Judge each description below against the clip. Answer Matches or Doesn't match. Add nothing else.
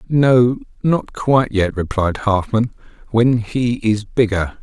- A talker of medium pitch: Doesn't match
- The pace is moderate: Doesn't match